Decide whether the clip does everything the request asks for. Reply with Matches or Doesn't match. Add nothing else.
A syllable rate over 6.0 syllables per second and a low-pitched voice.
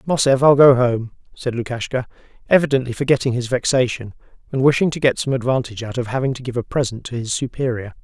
Matches